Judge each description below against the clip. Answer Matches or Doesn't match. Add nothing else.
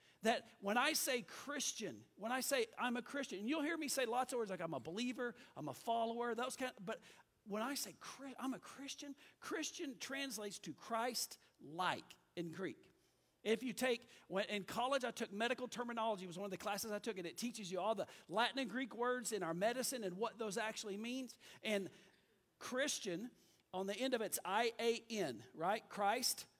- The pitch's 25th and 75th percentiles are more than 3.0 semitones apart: Matches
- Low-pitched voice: Doesn't match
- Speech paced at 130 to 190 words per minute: Doesn't match